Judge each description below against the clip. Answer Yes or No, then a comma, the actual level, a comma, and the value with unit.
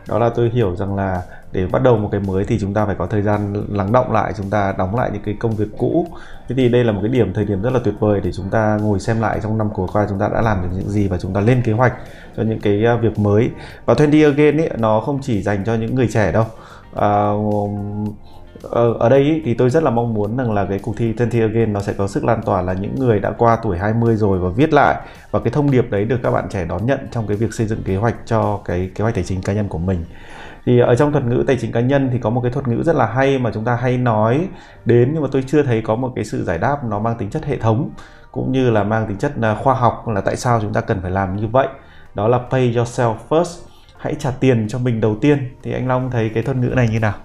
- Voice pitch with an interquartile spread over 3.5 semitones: No, average, 3.2 semitones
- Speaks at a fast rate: Yes, fast, 290 wpm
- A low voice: Yes, low, 115 Hz